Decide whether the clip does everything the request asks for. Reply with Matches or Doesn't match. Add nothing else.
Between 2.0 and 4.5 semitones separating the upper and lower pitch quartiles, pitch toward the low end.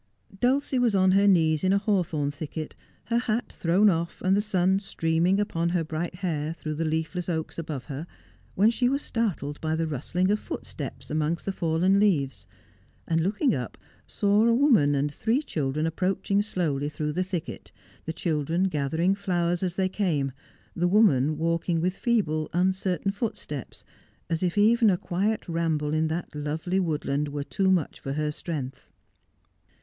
Doesn't match